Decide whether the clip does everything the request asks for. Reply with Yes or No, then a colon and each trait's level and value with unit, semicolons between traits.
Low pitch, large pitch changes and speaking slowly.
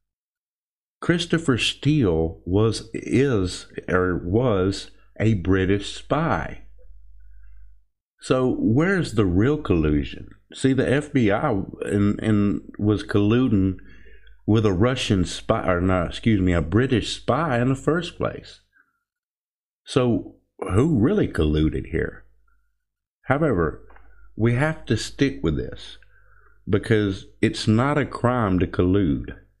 Yes: low, 105 Hz; wide, 5.7 semitones; slow, 110 wpm